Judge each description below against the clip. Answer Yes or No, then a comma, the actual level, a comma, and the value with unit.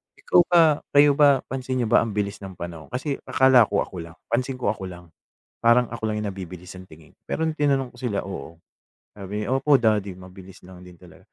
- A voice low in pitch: Yes, low, 105 Hz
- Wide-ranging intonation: Yes, wide, 6.0 semitones